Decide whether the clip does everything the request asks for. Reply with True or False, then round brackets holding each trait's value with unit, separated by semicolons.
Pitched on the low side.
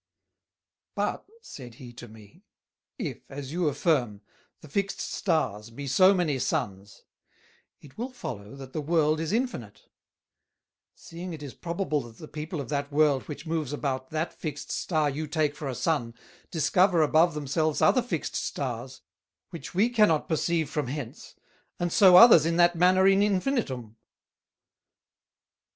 False (155 Hz)